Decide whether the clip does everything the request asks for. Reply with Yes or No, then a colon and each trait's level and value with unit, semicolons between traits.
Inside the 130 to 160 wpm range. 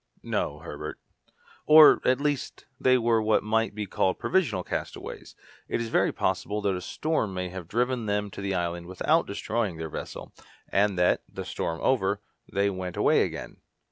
No: average, 170 wpm